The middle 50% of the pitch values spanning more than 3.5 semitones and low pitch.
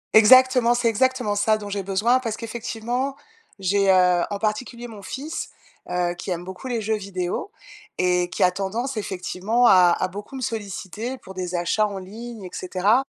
No: average, 4.2 semitones; high, 210 Hz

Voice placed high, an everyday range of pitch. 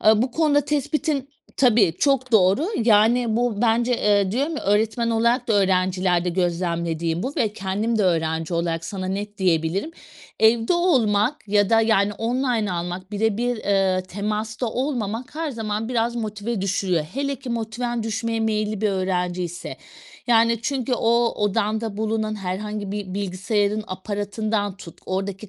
Yes: high, 215 Hz; average, 3.5 semitones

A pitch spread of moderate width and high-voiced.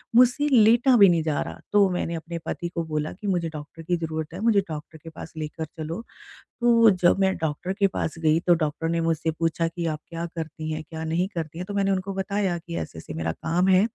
No: average, 3.3 semitones; medium, 170 Hz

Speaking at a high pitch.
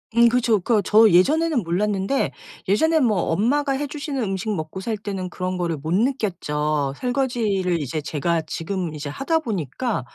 Yes: high, 200 Hz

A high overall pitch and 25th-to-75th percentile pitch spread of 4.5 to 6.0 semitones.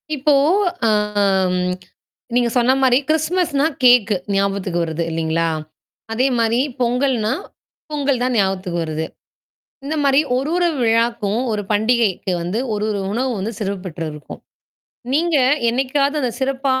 Yes: high, 235 Hz; average, 5.2 semitones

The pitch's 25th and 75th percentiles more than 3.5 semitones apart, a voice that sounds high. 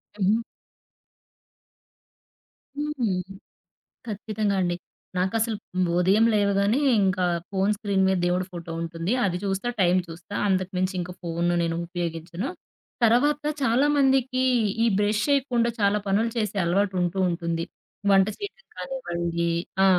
Yes: average, 4.5 semitones; high, 195 Hz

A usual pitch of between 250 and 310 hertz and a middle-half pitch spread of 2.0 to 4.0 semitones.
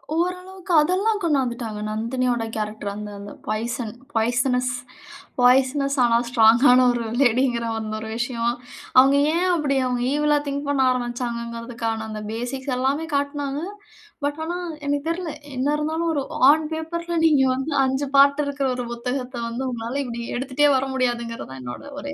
Yes: very high, 260 Hz; average, 3.6 semitones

